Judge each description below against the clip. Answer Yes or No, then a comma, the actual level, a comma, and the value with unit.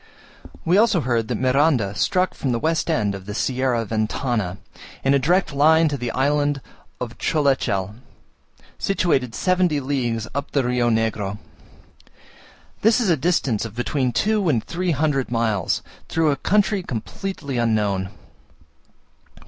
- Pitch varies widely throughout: Yes, wide, 5.9 semitones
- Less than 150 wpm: Yes, average, 140 wpm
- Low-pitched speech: Yes, low, 130 Hz